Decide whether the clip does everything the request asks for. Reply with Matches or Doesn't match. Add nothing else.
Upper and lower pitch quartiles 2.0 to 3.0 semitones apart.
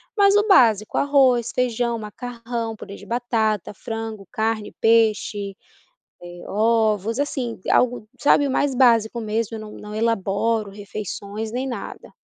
Matches